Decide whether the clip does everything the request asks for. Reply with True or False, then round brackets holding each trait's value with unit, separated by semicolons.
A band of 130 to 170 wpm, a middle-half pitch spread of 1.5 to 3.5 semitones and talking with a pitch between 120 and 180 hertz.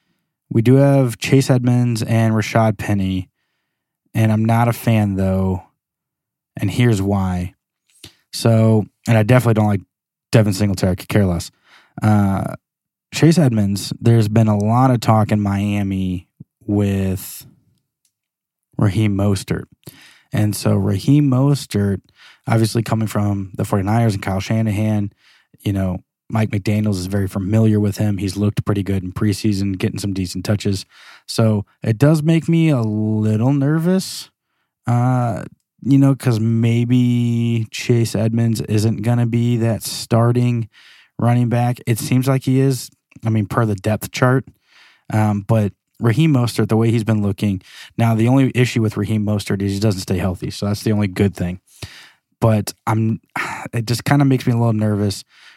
False (155 wpm; 2.9 semitones; 110 Hz)